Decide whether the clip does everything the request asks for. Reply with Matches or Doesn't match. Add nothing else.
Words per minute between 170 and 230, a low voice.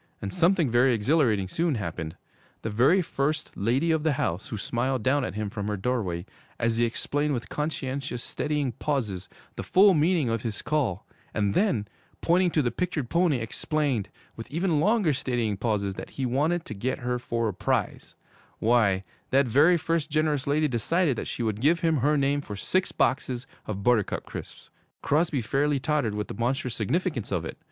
Matches